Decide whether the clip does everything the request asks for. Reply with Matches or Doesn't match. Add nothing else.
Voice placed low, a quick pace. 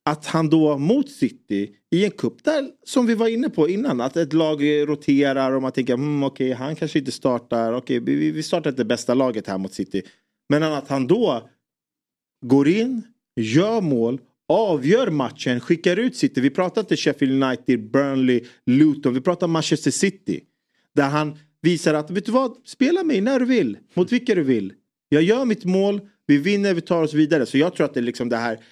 Doesn't match